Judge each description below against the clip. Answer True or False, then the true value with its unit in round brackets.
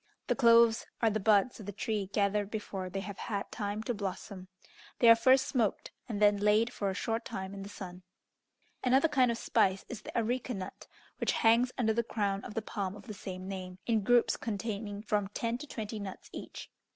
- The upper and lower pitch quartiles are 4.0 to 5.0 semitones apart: False (2.6 semitones)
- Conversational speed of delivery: False (210 wpm)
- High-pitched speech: True (210 Hz)